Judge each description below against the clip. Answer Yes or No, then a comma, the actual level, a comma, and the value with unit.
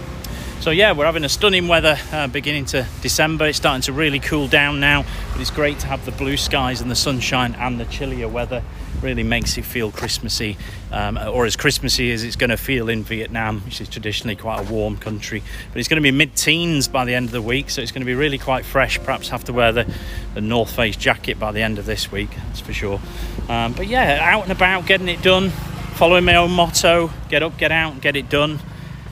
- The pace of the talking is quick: Yes, fast, 240 wpm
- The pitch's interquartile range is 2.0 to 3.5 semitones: No, average, 5.2 semitones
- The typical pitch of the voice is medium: No, low, 125 Hz